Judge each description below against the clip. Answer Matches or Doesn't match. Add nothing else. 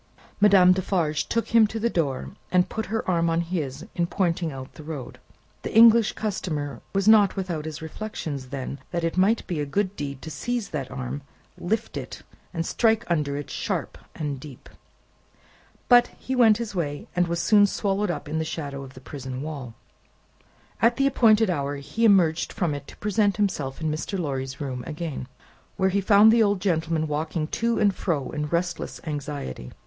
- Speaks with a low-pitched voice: Doesn't match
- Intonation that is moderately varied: Doesn't match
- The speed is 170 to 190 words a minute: Matches